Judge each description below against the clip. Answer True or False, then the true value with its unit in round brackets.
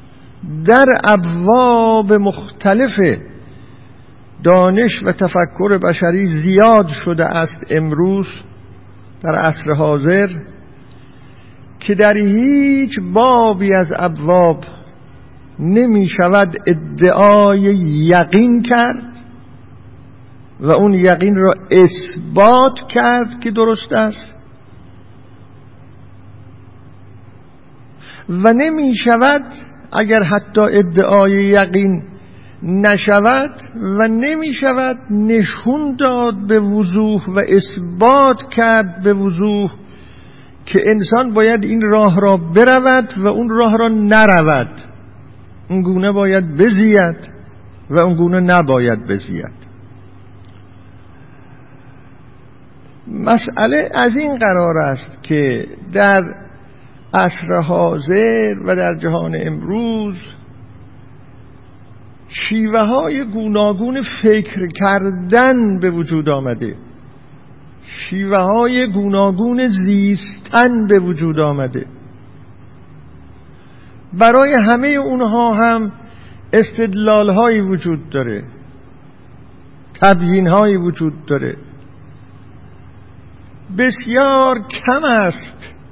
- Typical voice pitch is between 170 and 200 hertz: True (185 Hz)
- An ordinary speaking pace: False (80 wpm)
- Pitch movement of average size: False (8.7 semitones)